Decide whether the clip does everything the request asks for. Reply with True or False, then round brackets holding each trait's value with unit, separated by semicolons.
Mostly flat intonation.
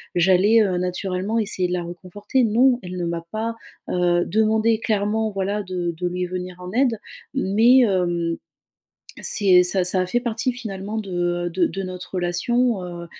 False (3.6 semitones)